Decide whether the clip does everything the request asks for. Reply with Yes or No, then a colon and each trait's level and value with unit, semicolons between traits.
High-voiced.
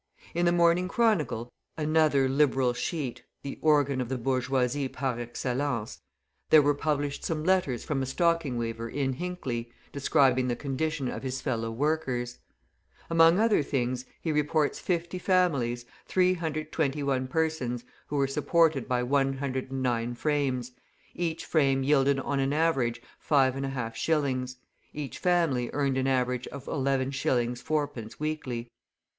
No: low, 135 Hz